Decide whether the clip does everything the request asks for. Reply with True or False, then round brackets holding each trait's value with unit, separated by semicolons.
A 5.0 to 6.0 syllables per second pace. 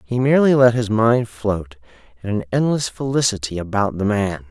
True (5.1 syllables/s)